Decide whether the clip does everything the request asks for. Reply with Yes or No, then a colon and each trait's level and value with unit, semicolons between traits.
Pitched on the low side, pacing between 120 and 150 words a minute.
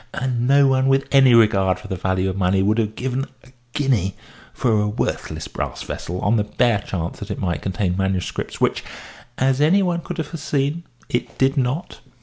No: low, 120 Hz; average, 195 wpm